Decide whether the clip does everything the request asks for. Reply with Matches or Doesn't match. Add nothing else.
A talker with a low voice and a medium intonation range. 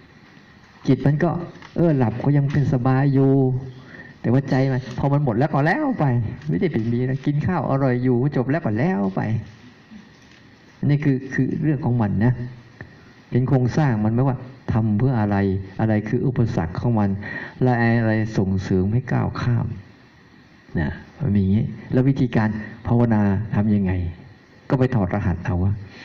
Matches